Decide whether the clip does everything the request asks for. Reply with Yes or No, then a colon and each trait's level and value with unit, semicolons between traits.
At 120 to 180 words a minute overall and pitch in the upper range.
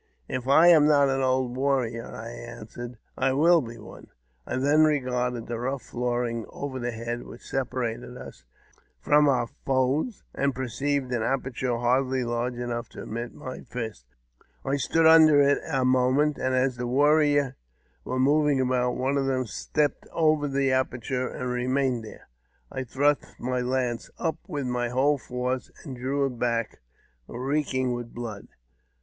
No: average, 160 wpm; low, 130 Hz